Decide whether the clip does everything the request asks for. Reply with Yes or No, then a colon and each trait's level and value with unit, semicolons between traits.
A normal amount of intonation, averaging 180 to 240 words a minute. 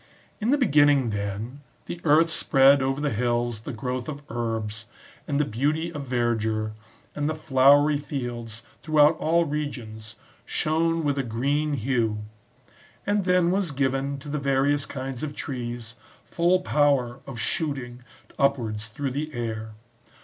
No: average, 4.0 semitones; average, 145 wpm